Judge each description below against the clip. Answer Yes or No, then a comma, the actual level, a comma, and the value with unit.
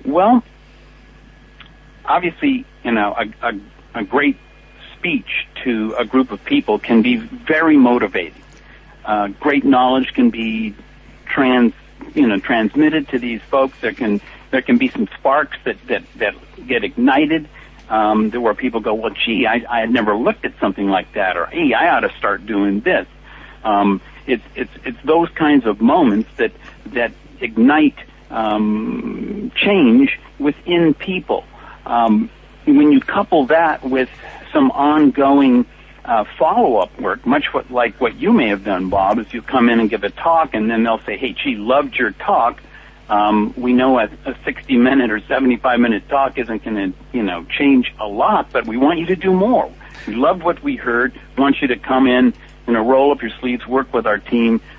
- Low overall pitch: Yes, low, 130 Hz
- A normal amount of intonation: No, wide, 6.5 semitones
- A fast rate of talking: No, average, 180 wpm